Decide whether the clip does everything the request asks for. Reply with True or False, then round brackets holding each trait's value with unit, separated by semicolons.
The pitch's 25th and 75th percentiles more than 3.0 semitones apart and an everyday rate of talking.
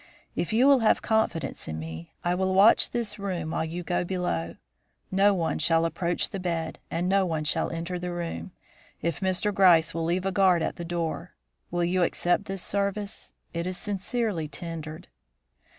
False (2.7 semitones; 180 wpm)